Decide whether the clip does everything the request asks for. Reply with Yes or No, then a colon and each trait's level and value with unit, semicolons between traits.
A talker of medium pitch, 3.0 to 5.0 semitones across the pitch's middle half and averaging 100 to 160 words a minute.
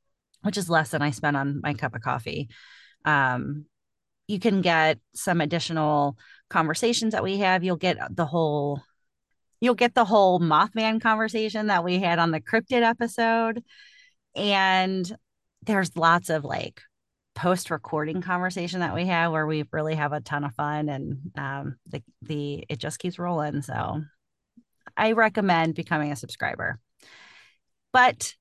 No: medium, 170 Hz; wide, 5.4 semitones; average, 150 wpm